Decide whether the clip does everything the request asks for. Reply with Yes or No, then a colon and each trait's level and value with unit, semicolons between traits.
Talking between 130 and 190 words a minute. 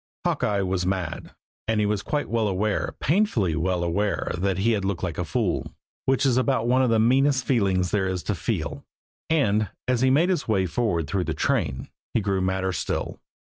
No: average, 200 wpm